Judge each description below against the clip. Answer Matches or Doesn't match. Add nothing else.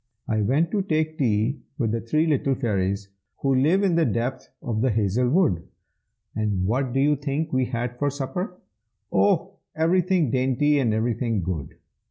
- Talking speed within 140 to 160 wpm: Doesn't match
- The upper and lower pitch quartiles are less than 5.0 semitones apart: Doesn't match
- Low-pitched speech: Matches